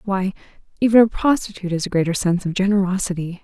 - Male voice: No, female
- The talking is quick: No, average, 175 wpm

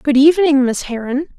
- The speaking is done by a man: No, female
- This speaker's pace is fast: No, average, 175 wpm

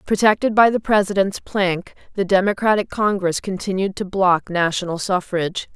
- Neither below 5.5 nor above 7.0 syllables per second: No, 5.0 syllables/s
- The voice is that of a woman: Yes, female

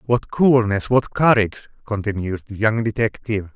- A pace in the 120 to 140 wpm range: Yes, slow, 135 wpm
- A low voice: Yes, low, 110 Hz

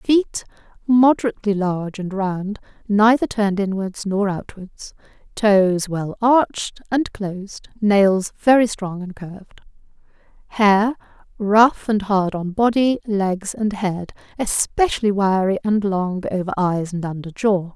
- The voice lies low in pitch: No, high, 205 Hz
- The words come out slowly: Yes, slow, 120 wpm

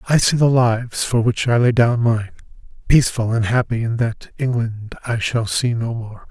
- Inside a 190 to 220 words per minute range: Yes, average, 200 wpm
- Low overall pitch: Yes, low, 115 Hz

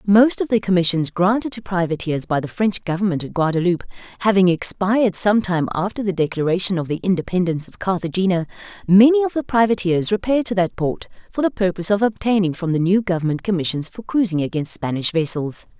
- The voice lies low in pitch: No, high, 190 Hz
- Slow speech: No, average, 180 wpm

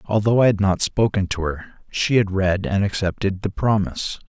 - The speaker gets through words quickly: No, average, 195 wpm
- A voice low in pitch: Yes, low, 100 Hz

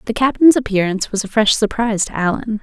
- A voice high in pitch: Yes, high, 220 Hz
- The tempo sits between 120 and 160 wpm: No, fast, 205 wpm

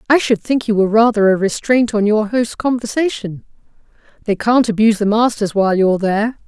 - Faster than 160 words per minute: Yes, average, 185 wpm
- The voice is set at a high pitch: Yes, high, 220 Hz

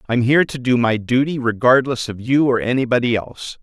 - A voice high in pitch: No, low, 125 Hz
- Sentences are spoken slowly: No, average, 200 wpm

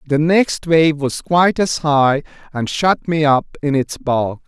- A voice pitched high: No, medium, 150 Hz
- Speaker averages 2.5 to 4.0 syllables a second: Yes, 3.9 syllables/s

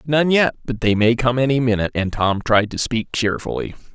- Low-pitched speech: Yes, low, 120 Hz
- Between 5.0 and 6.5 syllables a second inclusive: Yes, 5.5 syllables/s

